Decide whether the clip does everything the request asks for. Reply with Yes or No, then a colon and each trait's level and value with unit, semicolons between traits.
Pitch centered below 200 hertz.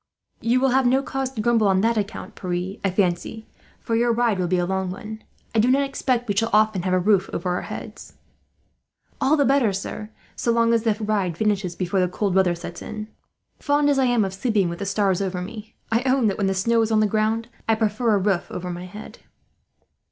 No: high, 215 Hz